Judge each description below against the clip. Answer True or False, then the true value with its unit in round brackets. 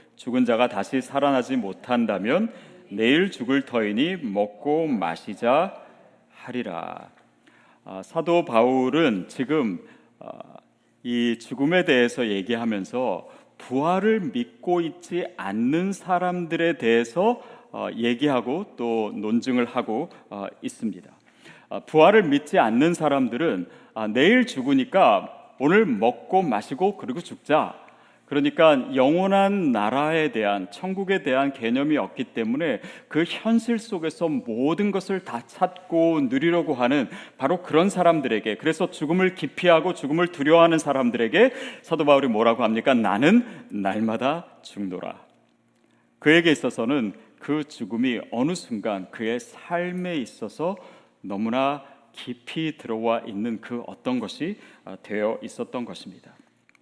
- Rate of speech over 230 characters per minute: True (270 characters per minute)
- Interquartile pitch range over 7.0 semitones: True (7.7 semitones)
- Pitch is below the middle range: False (160 Hz)